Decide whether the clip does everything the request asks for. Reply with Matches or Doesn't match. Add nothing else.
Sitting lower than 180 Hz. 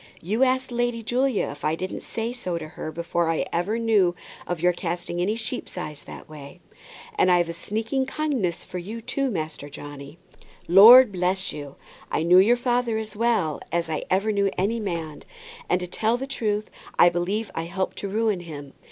Doesn't match